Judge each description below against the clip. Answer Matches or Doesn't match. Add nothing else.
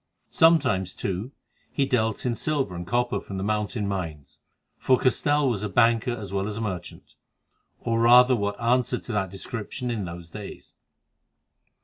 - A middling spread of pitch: Matches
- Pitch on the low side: Matches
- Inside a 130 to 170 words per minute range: Matches